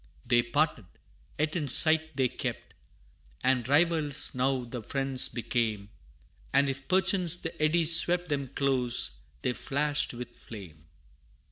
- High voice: No, low, 135 Hz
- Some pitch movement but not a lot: Yes, average, 4.4 semitones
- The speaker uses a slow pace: Yes, slow, 130 wpm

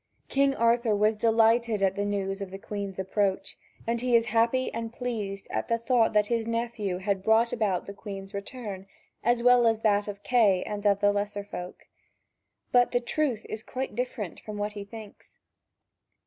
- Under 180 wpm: No, average, 185 wpm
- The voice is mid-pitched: No, high, 215 Hz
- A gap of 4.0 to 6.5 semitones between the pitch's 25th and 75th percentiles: No, average, 2.7 semitones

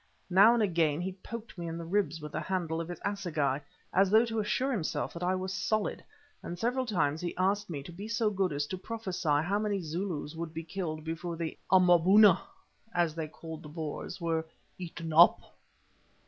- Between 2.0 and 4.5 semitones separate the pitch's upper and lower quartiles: Yes, average, 3.6 semitones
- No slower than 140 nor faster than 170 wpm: No, average, 200 wpm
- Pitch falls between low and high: Yes, medium, 175 Hz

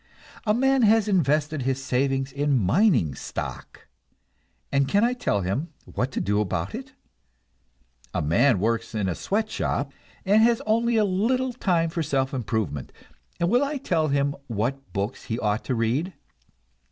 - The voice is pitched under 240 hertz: Yes, medium, 140 Hz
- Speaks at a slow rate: No, average, 160 wpm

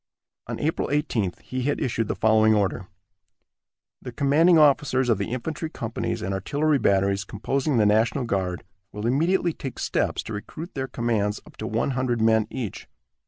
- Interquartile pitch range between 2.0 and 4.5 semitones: No, average, 5.0 semitones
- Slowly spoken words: No, average, 165 wpm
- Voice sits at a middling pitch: No, low, 120 Hz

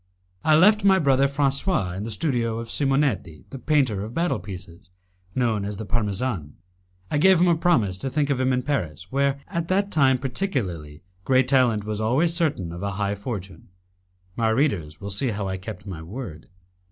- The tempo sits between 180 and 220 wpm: Yes, average, 190 wpm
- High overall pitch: No, low, 120 Hz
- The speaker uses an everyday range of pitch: No, wide, 6.2 semitones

